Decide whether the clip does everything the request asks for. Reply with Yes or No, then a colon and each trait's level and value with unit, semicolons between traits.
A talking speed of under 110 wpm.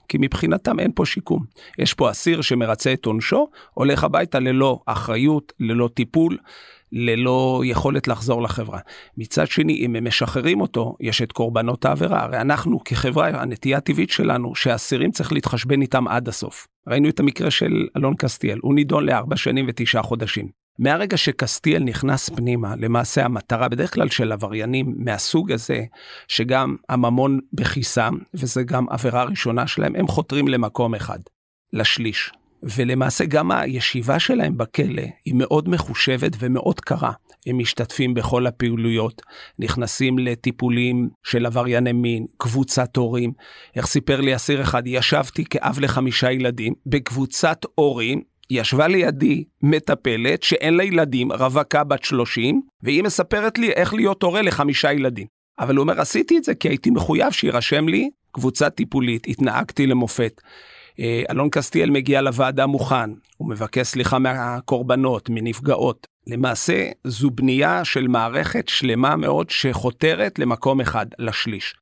No: average, 140 wpm